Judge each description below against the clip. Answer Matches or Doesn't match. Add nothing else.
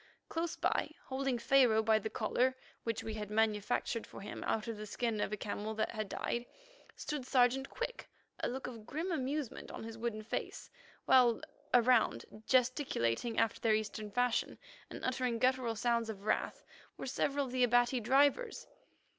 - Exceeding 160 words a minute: Matches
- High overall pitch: Matches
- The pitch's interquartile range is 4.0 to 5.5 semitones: Doesn't match